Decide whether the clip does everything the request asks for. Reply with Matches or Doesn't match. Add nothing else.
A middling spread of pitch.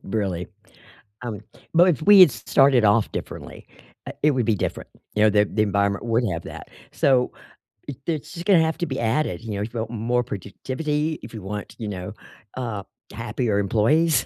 Doesn't match